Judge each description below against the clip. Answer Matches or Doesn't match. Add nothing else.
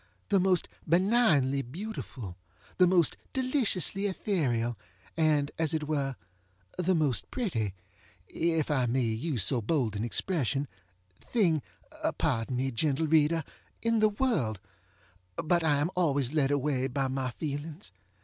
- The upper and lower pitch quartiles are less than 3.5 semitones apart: Doesn't match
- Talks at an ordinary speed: Doesn't match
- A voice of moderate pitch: Matches